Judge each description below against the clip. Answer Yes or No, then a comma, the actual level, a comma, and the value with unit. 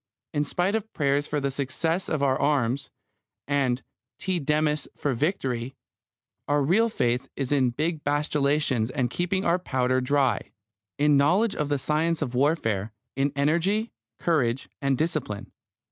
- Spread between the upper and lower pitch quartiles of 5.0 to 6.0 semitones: No, average, 3.5 semitones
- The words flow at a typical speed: Yes, average, 145 wpm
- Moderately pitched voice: Yes, medium, 145 Hz